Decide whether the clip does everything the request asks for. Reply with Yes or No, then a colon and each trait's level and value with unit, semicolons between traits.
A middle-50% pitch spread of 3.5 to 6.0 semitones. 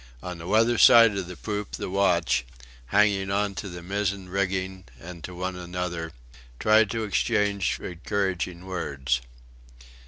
No: narrow, 2.4 semitones